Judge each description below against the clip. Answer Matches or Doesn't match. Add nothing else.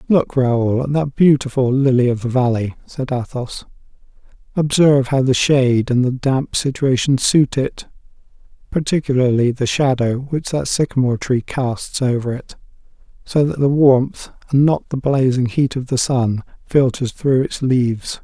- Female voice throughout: Doesn't match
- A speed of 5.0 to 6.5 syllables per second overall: Doesn't match